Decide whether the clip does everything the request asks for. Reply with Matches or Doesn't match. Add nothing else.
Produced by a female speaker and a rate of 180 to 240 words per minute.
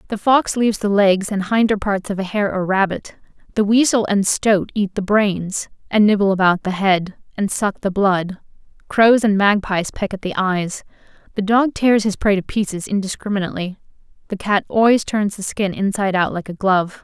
Matches